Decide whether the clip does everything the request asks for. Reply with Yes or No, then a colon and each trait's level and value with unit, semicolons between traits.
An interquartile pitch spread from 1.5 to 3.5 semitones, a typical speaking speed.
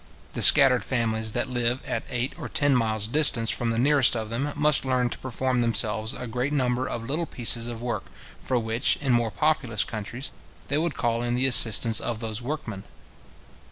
Yes: average, 2.7 semitones; average, 195 wpm